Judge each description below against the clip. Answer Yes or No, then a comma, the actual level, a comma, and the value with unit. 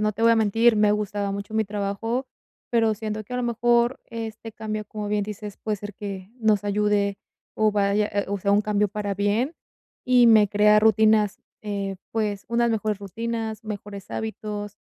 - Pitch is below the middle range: No, high, 210 Hz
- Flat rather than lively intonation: Yes, narrow, 1.5 semitones